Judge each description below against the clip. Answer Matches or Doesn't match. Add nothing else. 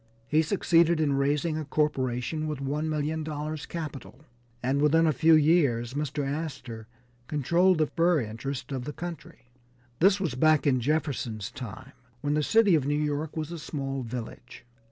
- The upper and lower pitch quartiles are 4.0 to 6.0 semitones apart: Doesn't match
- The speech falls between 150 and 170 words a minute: Matches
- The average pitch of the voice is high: Doesn't match